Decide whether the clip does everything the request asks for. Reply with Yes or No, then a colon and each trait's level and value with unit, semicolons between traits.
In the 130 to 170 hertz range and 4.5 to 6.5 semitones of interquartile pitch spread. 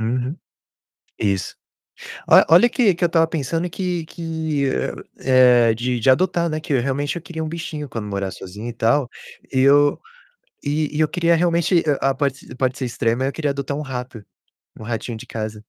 Yes: medium, 140 Hz; average, 5.1 semitones